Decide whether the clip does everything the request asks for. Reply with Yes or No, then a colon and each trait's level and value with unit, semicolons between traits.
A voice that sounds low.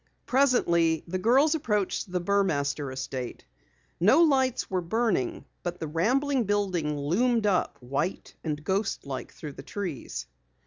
No: medium, 185 Hz